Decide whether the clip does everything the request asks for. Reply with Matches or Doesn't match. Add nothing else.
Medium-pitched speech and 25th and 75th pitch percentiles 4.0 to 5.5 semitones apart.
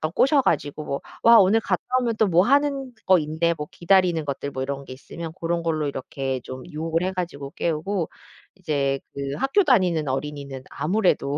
Matches